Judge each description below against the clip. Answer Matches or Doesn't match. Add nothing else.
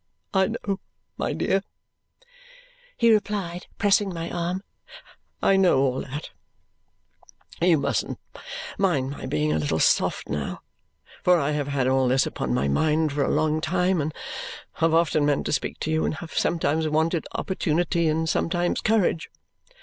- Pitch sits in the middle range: Matches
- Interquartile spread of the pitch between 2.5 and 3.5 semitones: Doesn't match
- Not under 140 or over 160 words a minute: Matches